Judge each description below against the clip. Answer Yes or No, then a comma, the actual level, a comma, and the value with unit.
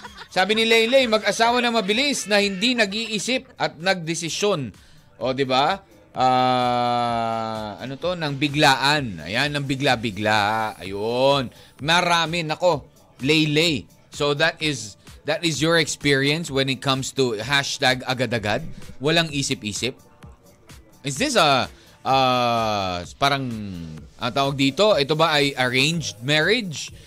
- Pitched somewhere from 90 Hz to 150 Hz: Yes, medium, 140 Hz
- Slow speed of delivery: No, average, 120 wpm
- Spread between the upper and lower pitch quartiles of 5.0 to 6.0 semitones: Yes, average, 5.3 semitones